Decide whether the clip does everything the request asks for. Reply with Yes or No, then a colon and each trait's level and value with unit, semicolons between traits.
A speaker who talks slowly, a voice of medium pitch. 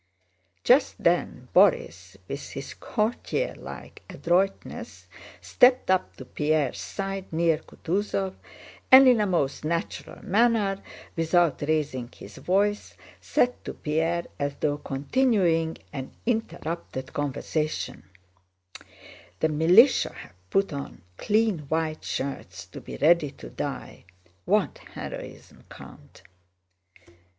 Yes: slow, 105 wpm; medium, 165 Hz